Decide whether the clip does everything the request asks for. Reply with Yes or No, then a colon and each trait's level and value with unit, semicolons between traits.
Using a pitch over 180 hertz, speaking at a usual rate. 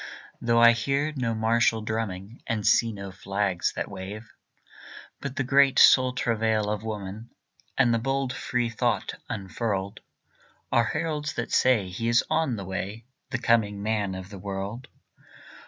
No: low, 115 Hz; average, 155 wpm